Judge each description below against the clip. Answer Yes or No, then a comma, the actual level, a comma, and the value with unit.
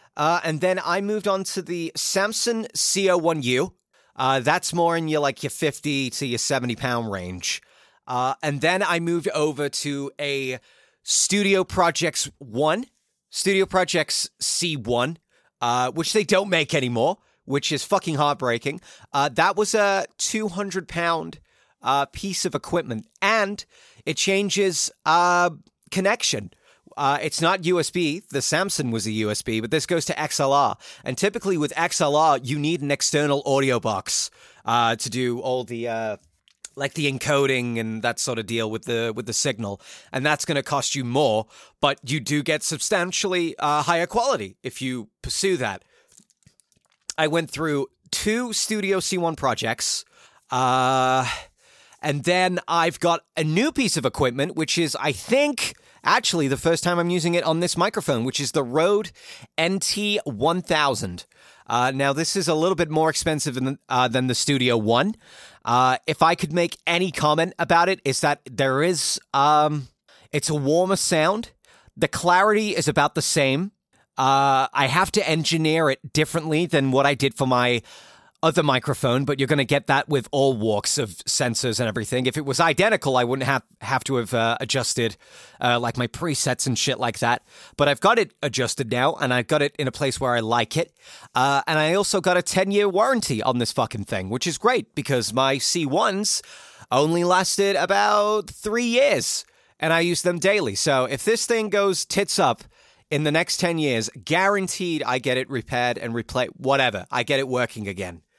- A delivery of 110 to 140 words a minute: No, average, 180 wpm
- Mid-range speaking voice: Yes, medium, 150 Hz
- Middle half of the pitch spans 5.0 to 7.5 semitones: Yes, average, 5.3 semitones